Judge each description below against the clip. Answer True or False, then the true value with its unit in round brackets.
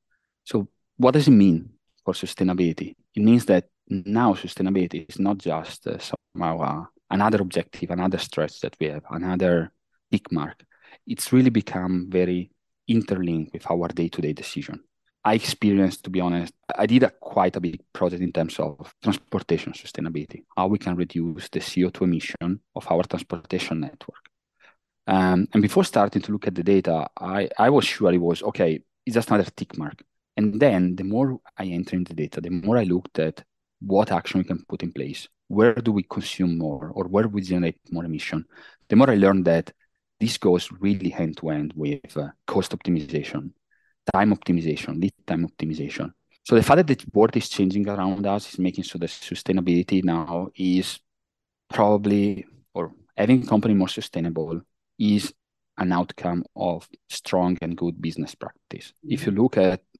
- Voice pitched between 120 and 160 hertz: False (90 Hz)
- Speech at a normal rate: True (175 wpm)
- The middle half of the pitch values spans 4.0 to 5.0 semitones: False (2.9 semitones)